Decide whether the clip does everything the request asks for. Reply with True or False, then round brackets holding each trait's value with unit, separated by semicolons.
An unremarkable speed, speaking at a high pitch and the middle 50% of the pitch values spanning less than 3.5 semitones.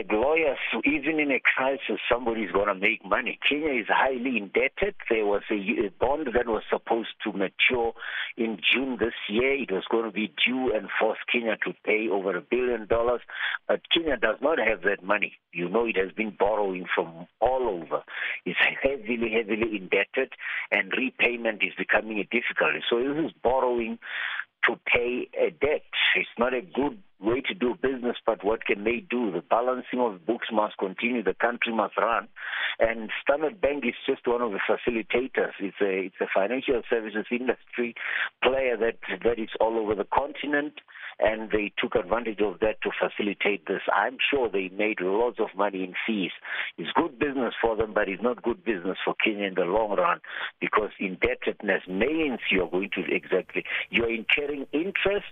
False (180 wpm; 115 Hz; 2.8 semitones)